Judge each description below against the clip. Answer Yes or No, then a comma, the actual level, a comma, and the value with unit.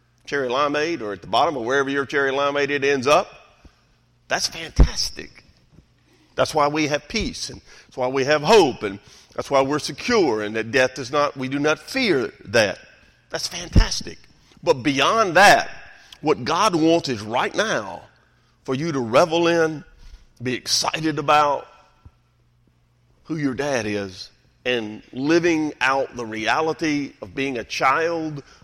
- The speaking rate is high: No, average, 155 wpm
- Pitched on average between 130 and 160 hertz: Yes, medium, 140 Hz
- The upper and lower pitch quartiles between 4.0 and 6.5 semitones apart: Yes, average, 4.4 semitones